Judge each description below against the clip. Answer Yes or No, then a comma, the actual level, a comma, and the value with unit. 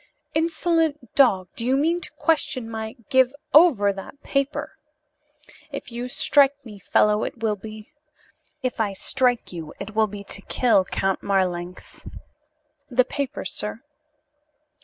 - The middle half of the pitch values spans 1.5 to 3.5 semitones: No, wide, 5.5 semitones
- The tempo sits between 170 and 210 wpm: No, average, 145 wpm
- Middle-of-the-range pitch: No, high, 240 Hz